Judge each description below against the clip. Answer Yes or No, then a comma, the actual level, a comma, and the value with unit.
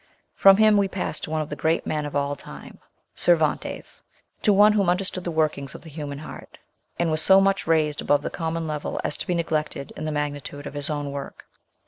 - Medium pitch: Yes, medium, 155 Hz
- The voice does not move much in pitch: No, average, 3.3 semitones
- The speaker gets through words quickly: Yes, fast, 225 wpm